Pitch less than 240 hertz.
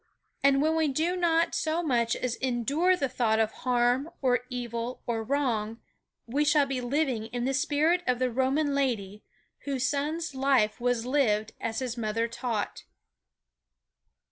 No: very high, 255 Hz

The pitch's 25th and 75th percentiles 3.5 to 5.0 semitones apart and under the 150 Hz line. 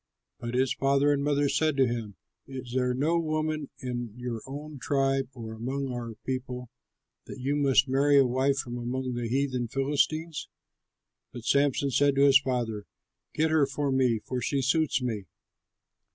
No: narrow, 2.4 semitones; low, 135 Hz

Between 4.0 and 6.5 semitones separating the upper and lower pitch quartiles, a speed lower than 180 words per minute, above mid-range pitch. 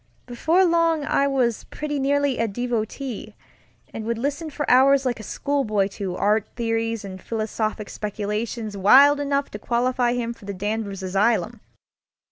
Yes: average, 4.6 semitones; average, 150 wpm; high, 235 Hz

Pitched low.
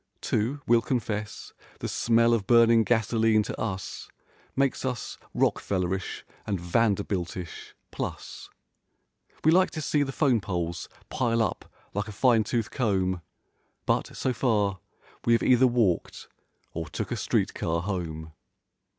Yes: low, 110 Hz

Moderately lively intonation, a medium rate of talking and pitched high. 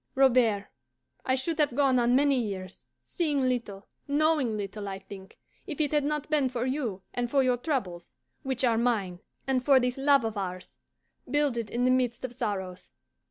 Yes: average, 4.9 semitones; average, 180 wpm; very high, 250 Hz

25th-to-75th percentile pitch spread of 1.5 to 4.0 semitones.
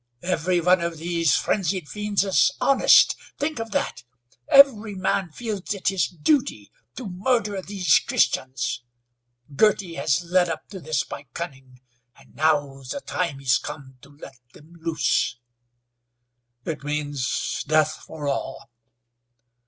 No: average, 5.3 semitones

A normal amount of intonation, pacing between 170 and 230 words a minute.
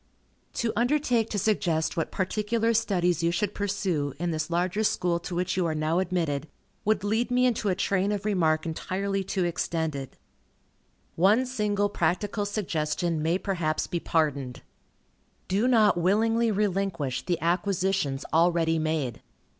No: average, 4.2 semitones; average, 145 wpm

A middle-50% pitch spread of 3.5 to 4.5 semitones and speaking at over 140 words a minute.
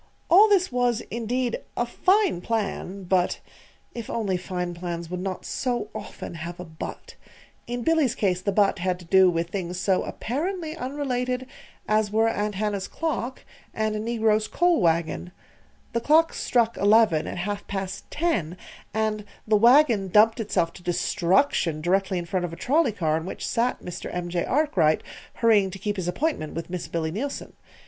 No: average, 5.2 semitones; average, 170 wpm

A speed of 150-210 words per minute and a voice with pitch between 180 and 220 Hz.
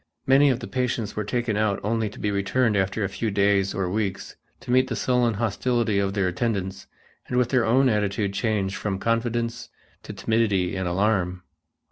No: average, 185 wpm; low, 105 Hz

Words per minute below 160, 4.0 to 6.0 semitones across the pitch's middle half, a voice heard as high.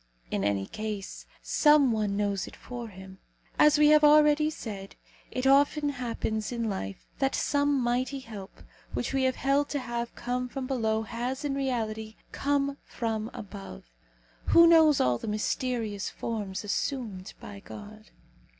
Yes: average, 150 wpm; average, 4.7 semitones; high, 240 Hz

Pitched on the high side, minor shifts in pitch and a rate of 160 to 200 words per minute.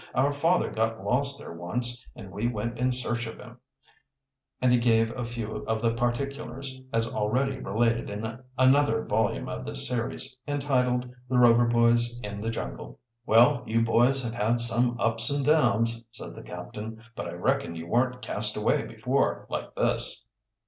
No: low, 120 Hz; narrow, 2.0 semitones; average, 170 wpm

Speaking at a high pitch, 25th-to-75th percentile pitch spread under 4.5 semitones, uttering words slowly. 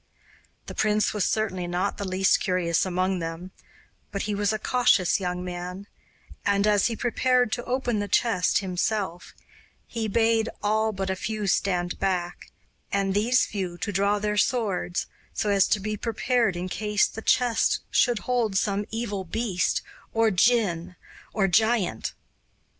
No: high, 200 Hz; average, 3.1 semitones; average, 155 wpm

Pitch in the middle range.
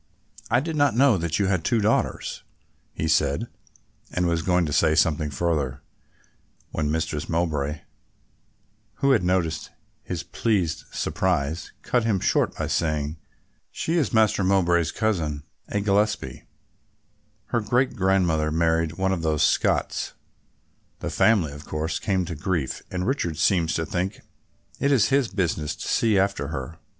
No: very low, 85 Hz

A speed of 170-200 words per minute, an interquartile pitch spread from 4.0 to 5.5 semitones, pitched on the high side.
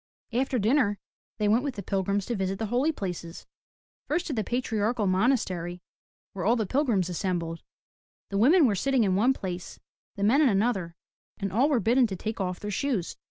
Yes: average, 195 wpm; average, 4.7 semitones; high, 210 Hz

